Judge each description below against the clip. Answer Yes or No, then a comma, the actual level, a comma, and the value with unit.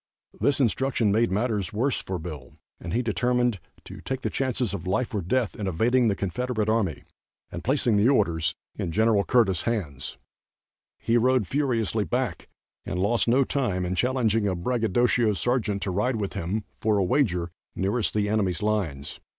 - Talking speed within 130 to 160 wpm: No, average, 170 wpm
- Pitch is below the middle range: Yes, low, 110 Hz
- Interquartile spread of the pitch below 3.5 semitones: No, average, 4.5 semitones